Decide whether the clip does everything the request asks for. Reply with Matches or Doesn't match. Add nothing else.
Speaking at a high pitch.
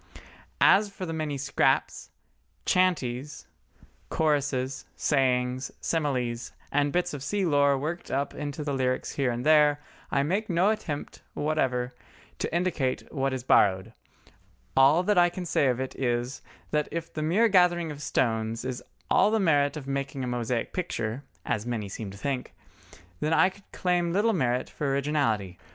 Doesn't match